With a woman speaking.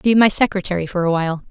Yes: female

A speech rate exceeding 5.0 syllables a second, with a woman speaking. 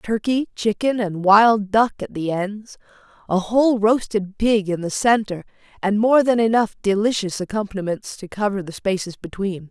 No: 4.8 syllables/s; female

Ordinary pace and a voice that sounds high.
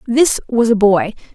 Yes: average, 180 wpm; high, 225 Hz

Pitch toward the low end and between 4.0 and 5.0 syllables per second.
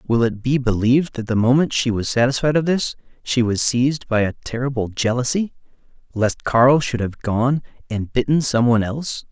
No: low, 125 Hz; 5.2 syllables/s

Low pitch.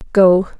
No: medium, 185 Hz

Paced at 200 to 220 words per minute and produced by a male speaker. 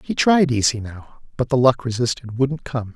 Yes: fast, 205 wpm; male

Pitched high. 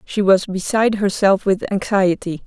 Yes: high, 195 Hz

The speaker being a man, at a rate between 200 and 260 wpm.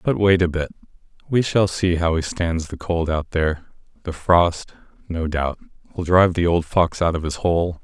Yes: male; fast, 205 wpm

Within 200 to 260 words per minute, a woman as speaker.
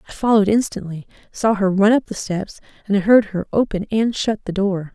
Yes: fast, 205 wpm; female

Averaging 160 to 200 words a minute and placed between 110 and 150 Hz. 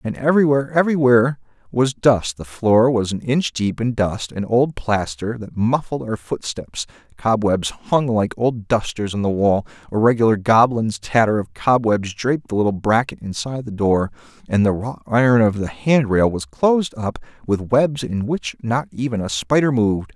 Yes: average, 180 wpm; low, 115 Hz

